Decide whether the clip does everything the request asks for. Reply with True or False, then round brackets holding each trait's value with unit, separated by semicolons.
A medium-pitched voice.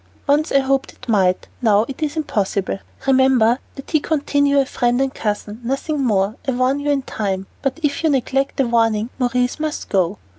False (260 Hz)